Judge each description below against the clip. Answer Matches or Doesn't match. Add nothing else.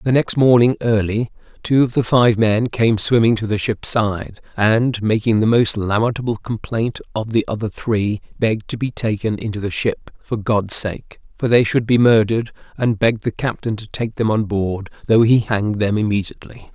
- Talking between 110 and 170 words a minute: Doesn't match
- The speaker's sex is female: Doesn't match